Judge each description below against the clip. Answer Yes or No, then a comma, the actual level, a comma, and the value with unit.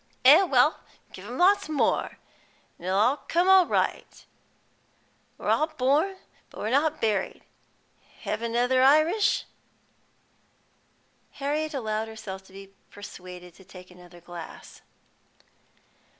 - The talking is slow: Yes, slow, 115 wpm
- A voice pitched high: Yes, very high, 250 Hz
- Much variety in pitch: Yes, wide, 8.2 semitones